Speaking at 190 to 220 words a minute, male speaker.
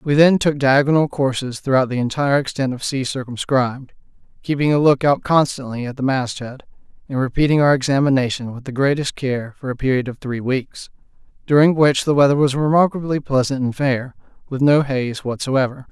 No: average, 175 wpm; male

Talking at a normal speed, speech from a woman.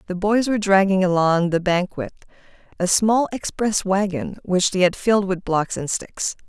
Yes: average, 175 wpm; female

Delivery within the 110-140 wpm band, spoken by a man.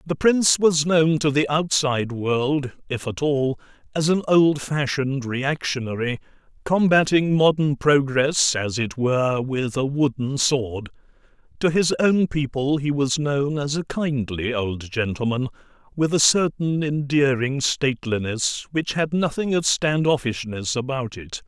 Yes: slow, 135 wpm; male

